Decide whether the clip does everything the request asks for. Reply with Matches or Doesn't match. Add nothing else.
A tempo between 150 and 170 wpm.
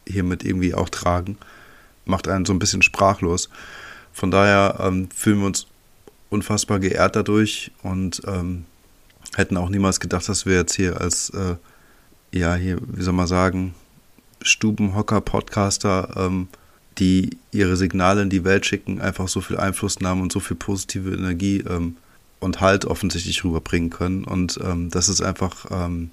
Matches